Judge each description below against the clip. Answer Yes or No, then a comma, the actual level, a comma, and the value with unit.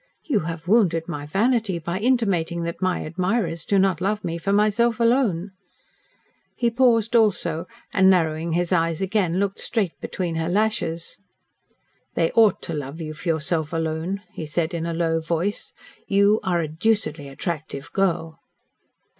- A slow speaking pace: No, average, 155 wpm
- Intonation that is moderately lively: Yes, average, 4.0 semitones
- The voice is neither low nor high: Yes, medium, 175 Hz